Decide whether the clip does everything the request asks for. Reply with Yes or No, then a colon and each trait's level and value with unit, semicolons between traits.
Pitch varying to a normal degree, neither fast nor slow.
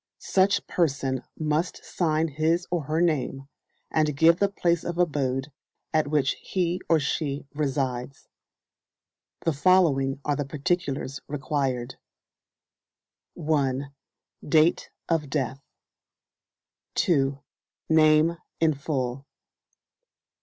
No: average, 3.2 semitones; slow, 100 wpm